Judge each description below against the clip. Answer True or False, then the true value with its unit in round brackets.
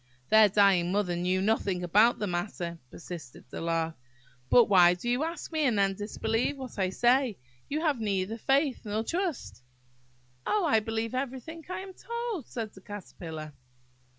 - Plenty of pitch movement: True (6.3 semitones)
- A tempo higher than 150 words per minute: True (165 wpm)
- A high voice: True (215 Hz)